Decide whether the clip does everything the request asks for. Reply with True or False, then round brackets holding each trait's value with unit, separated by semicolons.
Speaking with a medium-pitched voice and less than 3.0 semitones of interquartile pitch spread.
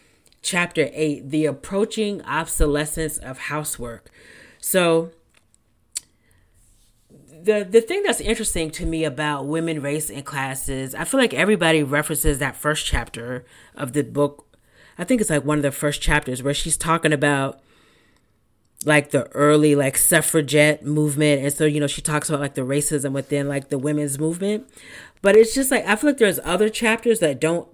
True (150 Hz; 2.6 semitones)